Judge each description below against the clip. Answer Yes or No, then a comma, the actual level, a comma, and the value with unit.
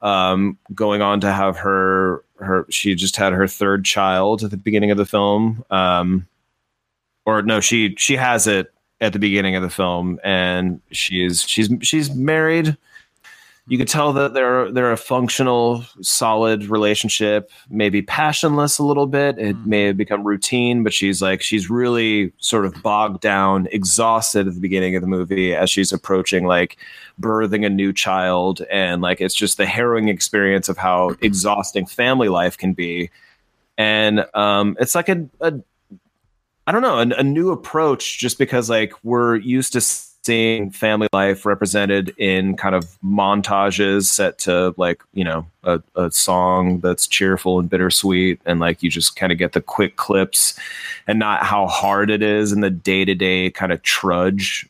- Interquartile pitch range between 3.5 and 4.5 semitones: No, average, 3.1 semitones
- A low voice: Yes, low, 100 Hz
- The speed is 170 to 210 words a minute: Yes, average, 175 wpm